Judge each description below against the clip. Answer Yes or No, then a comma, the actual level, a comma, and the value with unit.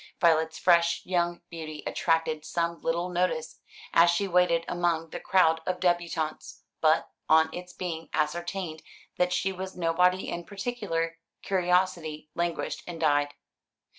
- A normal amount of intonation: No, narrow, 1.9 semitones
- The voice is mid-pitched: Yes, medium, 170 Hz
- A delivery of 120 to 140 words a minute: Yes, slow, 135 wpm